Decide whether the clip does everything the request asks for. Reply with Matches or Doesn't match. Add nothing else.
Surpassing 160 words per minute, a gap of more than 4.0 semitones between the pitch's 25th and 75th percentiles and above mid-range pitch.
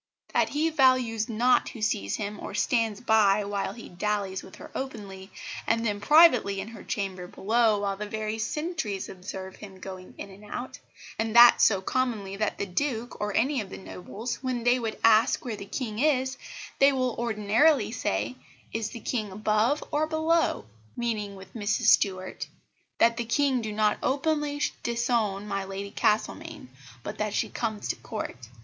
Doesn't match